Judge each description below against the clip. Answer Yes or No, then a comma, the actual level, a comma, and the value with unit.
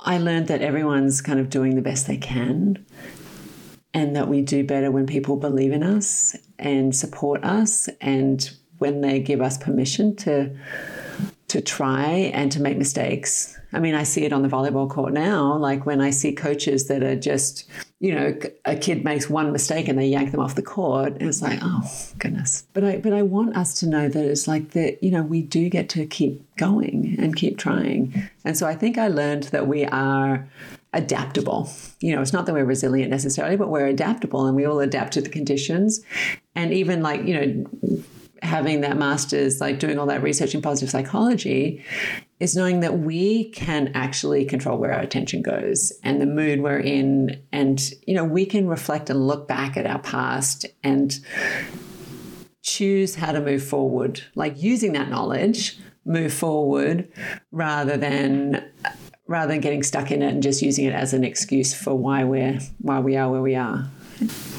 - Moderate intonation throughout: Yes, average, 3.7 semitones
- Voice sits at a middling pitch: Yes, medium, 145 Hz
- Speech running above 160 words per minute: Yes, average, 190 wpm